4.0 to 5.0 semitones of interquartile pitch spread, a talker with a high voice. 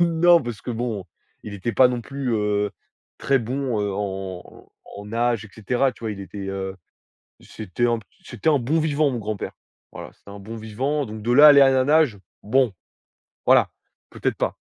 No: average, 4.7 semitones; low, 115 Hz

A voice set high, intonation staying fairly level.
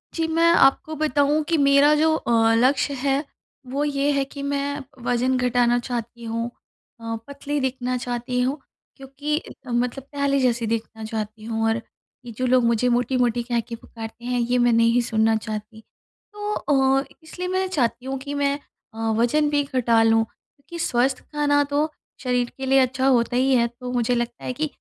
No: very high, 255 Hz; average, 3.1 semitones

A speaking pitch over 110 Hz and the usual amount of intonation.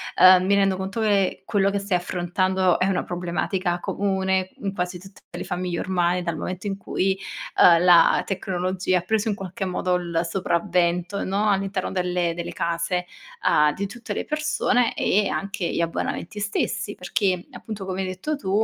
No: medium, 185 Hz; narrow, 1.9 semitones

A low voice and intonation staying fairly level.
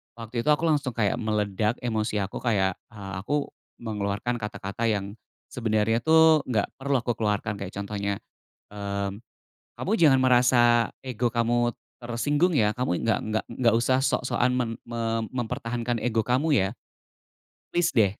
No: low, 115 Hz; average, 3.1 semitones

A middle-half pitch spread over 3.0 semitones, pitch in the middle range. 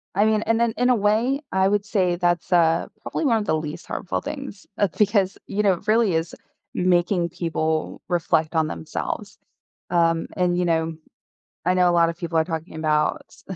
Yes: average, 4.0 semitones; medium, 180 Hz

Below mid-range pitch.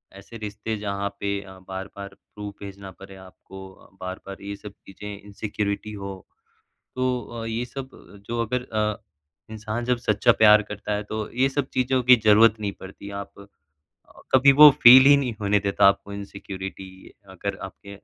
Yes: low, 105 Hz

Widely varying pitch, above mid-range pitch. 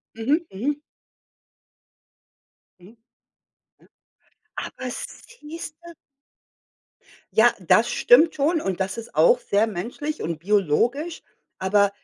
Yes: wide, 7.4 semitones; high, 235 Hz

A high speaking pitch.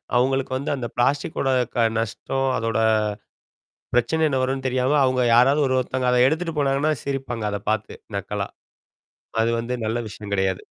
No: low, 130 Hz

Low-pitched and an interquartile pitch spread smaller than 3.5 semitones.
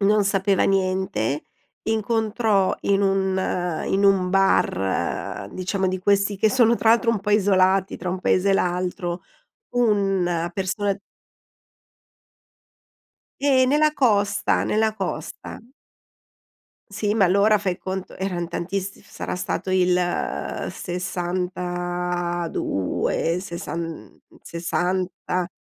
No: high, 190 Hz; narrow, 2.4 semitones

